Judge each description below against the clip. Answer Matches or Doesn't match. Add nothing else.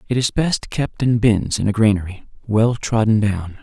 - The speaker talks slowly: Doesn't match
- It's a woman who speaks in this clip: Doesn't match